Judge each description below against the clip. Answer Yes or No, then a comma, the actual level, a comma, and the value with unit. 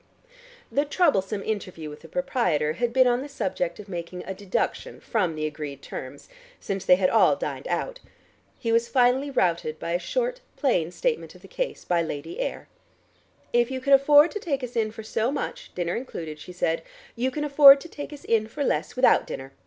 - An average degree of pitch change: No, wide, 8.0 semitones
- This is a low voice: No, high, 225 Hz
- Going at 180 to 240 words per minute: Yes, average, 200 wpm